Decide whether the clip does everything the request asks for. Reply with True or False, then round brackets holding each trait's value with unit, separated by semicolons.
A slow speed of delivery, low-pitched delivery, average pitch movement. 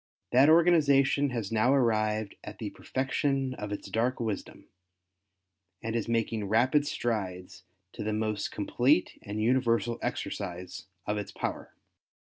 True (130 wpm; 115 Hz; 3.7 semitones)